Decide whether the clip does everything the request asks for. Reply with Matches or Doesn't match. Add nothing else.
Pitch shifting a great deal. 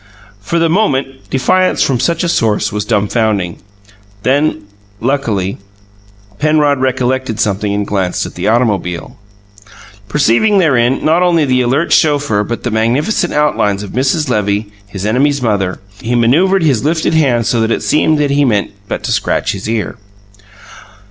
Matches